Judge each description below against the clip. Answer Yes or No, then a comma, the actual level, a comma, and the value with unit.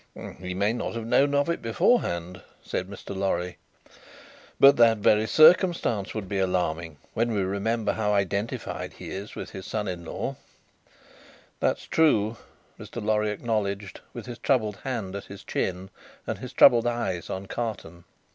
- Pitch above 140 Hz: No, low, 105 Hz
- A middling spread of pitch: Yes, average, 3.6 semitones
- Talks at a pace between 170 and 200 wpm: No, average, 155 wpm